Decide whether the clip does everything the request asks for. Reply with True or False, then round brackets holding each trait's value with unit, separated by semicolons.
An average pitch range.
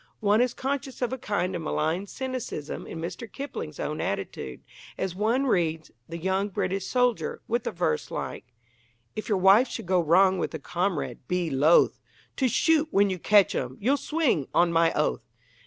False (6.1 semitones)